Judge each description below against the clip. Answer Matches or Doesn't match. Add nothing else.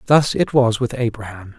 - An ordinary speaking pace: Matches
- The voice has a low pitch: Matches